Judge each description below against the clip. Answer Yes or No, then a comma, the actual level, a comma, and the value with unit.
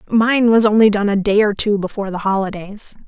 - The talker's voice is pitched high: Yes, high, 205 Hz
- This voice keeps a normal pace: No, fast, 215 wpm